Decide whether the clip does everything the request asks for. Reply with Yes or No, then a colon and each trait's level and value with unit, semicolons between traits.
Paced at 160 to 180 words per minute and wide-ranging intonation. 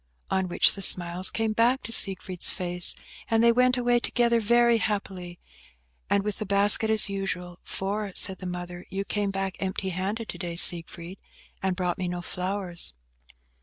No: average, 170 wpm; average, 3.3 semitones